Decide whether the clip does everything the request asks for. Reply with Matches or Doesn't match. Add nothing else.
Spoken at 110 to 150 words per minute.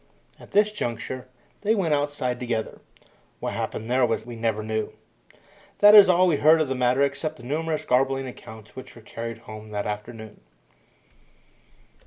Doesn't match